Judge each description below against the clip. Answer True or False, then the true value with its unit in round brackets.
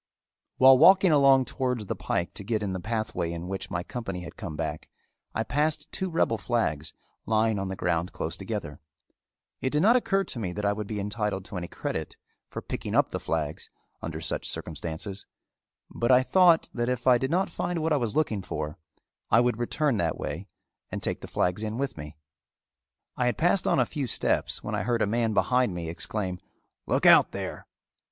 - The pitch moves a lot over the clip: True (6.6 semitones)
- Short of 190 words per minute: False (205 wpm)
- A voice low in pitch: True (110 Hz)